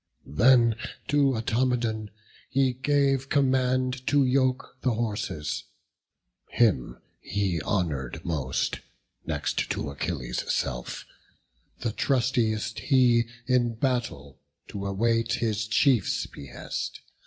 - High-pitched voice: No, low, 115 Hz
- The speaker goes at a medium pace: No, slow, 95 wpm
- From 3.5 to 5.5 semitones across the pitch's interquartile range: Yes, average, 4.6 semitones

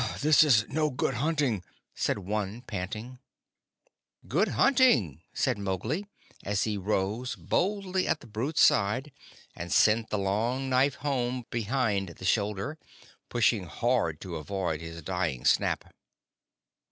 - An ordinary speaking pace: No, slow, 130 wpm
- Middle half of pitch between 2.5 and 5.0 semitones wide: No, wide, 5.5 semitones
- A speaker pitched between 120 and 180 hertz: No, low, 110 Hz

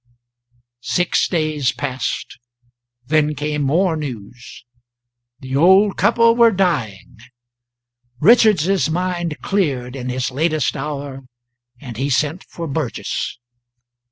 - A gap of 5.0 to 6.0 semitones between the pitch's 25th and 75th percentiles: Yes, average, 5.3 semitones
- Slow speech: Yes, slow, 100 wpm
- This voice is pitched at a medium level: Yes, medium, 150 Hz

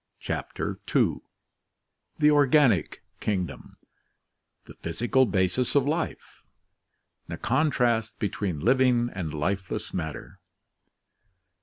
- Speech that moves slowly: Yes, slow, 75 wpm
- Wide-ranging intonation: Yes, wide, 6.2 semitones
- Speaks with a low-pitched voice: Yes, low, 115 Hz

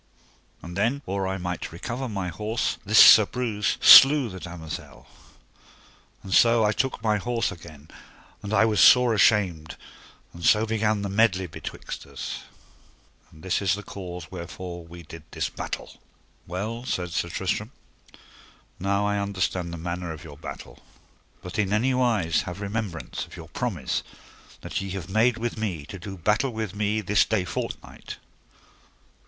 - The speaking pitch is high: No, low, 100 Hz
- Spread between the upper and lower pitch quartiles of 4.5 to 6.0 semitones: No, average, 3.9 semitones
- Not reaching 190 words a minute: Yes, average, 160 wpm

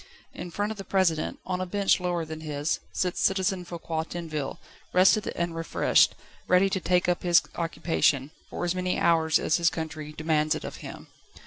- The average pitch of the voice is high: No, medium, 170 Hz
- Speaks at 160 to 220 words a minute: Yes, average, 185 wpm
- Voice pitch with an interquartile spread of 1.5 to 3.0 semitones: Yes, narrow, 2.5 semitones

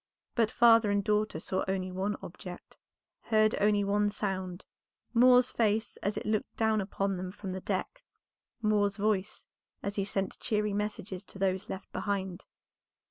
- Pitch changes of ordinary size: No, narrow, 1.9 semitones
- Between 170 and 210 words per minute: No, average, 155 wpm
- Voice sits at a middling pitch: No, high, 205 Hz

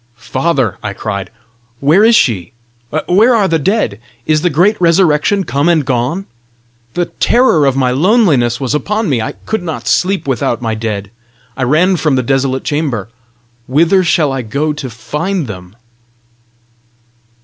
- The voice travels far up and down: Yes, wide, 6.5 semitones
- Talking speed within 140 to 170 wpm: Yes, average, 155 wpm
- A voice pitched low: No, medium, 145 Hz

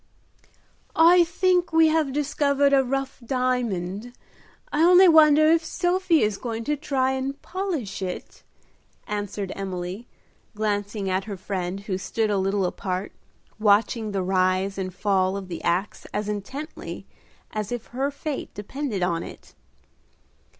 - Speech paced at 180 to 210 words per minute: No, average, 140 wpm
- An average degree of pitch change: No, wide, 6.7 semitones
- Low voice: No, high, 220 Hz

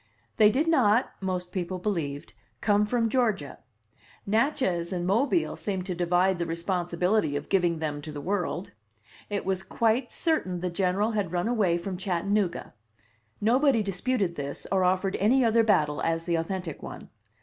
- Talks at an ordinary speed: Yes, average, 160 wpm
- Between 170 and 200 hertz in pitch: Yes, high, 190 Hz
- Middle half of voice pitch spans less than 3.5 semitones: No, average, 3.8 semitones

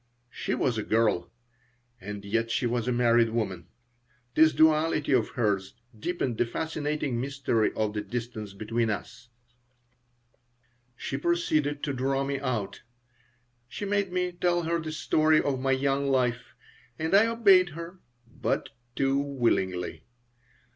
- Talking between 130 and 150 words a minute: Yes, average, 140 wpm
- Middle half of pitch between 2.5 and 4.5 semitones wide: No, average, 5.3 semitones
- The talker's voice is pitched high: No, low, 135 Hz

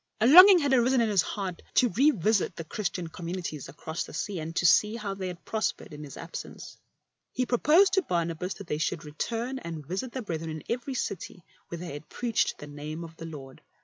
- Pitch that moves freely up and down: Yes, wide, 6.5 semitones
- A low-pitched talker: No, medium, 185 Hz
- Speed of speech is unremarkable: No, fast, 215 wpm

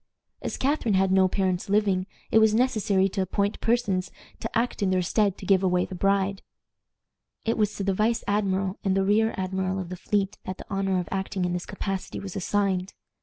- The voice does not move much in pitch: Yes, narrow, 1.7 semitones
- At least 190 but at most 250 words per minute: Yes, fast, 205 wpm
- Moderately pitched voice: No, high, 195 Hz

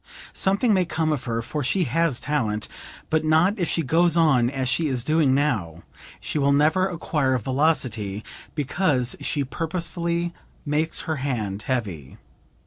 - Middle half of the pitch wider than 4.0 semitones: Yes, average, 4.8 semitones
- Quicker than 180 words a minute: No, average, 150 wpm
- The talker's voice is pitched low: No, medium, 150 Hz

